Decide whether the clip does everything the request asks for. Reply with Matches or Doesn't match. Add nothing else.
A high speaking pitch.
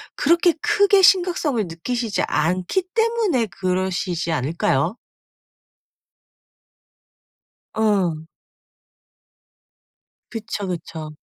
Matches